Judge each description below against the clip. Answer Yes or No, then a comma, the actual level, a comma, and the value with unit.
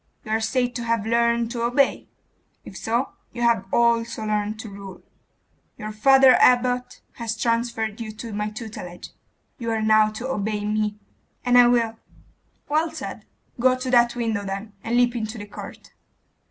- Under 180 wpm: Yes, average, 165 wpm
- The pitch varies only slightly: Yes, narrow, 2.1 semitones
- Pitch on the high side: Yes, high, 230 Hz